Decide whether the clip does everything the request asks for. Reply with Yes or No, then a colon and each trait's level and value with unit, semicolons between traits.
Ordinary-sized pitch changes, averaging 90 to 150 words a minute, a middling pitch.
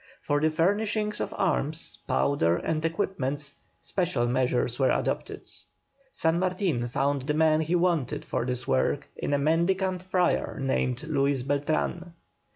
Yes: average, 4.6 semitones; average, 140 wpm; medium, 155 Hz